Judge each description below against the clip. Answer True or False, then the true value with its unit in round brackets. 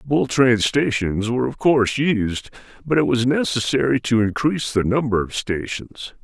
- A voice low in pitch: True (125 Hz)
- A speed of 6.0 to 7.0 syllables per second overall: False (5.0 syllables/s)